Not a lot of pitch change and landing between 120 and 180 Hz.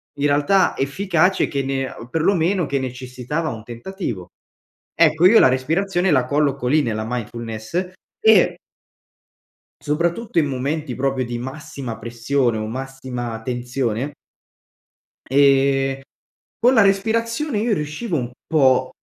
No: average, 5.3 semitones; medium, 140 Hz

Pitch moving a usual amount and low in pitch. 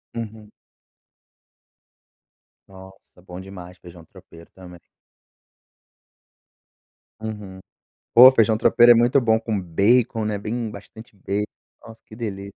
Yes: average, 3.2 semitones; low, 105 Hz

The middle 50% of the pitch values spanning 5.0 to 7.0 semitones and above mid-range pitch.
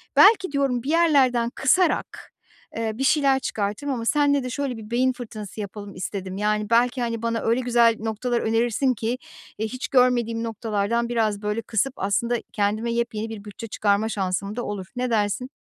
No: average, 3.1 semitones; high, 230 Hz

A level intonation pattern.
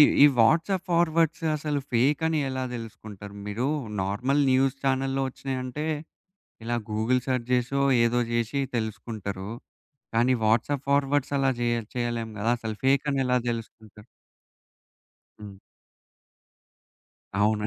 No: average, 3.6 semitones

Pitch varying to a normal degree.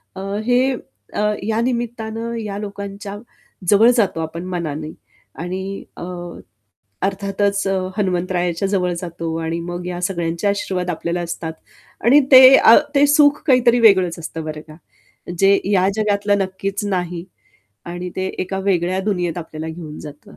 Yes: average, 3.1 semitones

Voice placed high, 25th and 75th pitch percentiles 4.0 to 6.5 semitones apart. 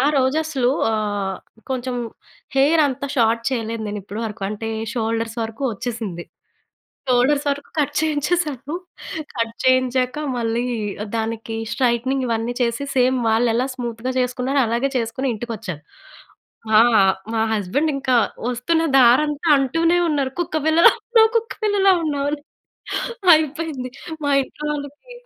Yes: very high, 255 Hz; average, 4.3 semitones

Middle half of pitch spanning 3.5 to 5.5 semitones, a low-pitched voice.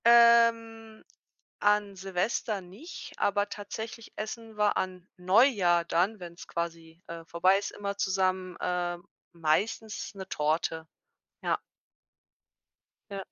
No: average, 3.8 semitones; high, 195 Hz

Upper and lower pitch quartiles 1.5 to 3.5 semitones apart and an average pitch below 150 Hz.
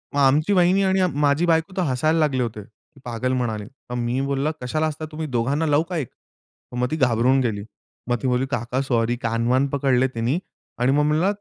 No: average, 4.2 semitones; low, 135 Hz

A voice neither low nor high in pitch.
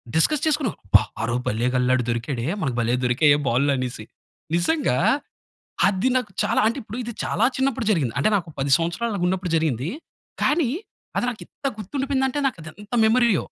Yes: medium, 175 Hz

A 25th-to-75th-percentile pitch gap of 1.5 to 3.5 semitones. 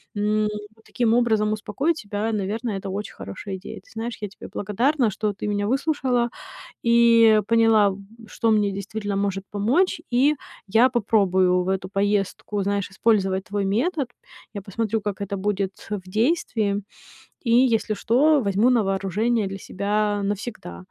Yes: average, 2.7 semitones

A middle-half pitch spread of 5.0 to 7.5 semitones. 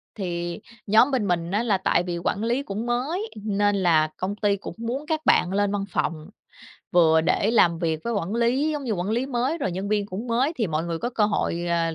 Yes: wide, 5.5 semitones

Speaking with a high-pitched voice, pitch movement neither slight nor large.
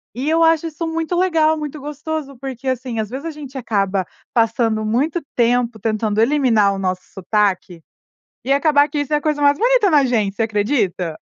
No: very high, 260 Hz; wide, 5.8 semitones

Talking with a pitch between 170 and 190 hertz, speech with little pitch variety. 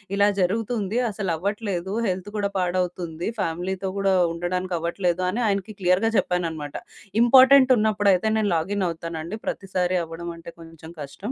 No: medium, 185 Hz; average, 3.0 semitones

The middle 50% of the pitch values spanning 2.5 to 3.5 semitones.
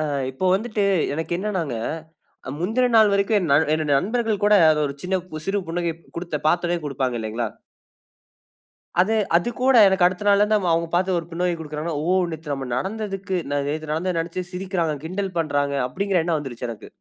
No: average, 4.1 semitones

